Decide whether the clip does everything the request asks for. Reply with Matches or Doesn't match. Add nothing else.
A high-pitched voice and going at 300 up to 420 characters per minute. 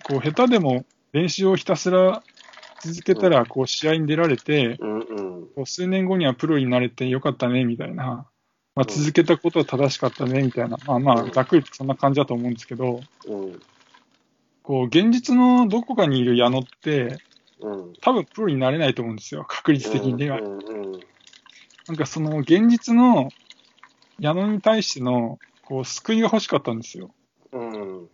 Doesn't match